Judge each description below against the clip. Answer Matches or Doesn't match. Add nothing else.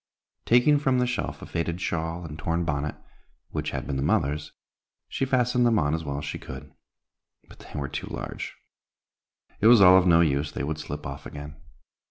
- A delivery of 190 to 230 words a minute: Matches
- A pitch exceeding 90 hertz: Doesn't match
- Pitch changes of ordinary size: Doesn't match